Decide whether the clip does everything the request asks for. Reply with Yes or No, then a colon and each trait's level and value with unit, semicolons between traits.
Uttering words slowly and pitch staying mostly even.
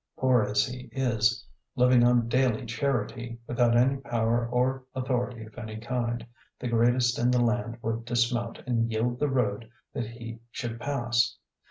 No: average, 160 wpm; narrow, 1.3 semitones